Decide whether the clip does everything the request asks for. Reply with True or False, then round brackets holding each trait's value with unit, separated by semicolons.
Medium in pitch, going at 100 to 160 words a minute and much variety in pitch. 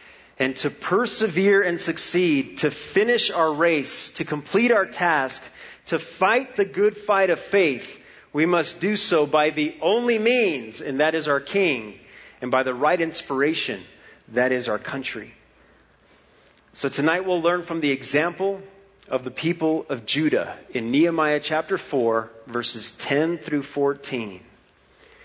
True (160 Hz; 145 wpm; 5.7 semitones)